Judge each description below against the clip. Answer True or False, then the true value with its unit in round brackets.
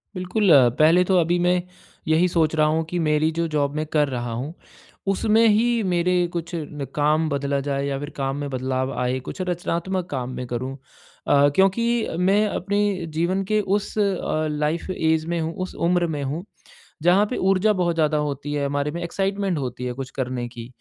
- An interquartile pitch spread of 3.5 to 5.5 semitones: True (4.3 semitones)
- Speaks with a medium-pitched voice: True (160 Hz)